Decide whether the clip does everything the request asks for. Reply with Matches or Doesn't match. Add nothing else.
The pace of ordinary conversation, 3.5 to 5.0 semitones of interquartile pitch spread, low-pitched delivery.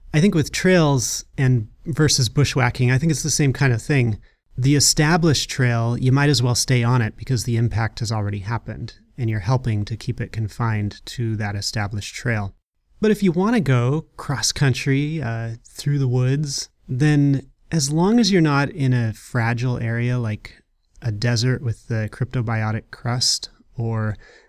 Matches